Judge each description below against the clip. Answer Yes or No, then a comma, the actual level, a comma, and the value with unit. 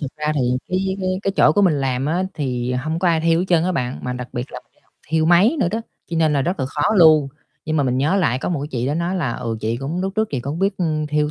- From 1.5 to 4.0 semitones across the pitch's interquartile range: No, average, 5.0 semitones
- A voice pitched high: No, medium, 155 Hz